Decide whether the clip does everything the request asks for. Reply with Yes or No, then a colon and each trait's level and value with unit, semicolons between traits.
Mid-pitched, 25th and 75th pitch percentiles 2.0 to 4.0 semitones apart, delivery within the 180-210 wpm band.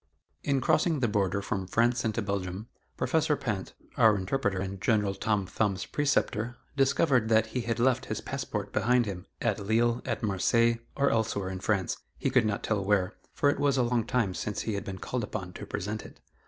No: low, 110 Hz; average, 3.6 semitones; average, 195 wpm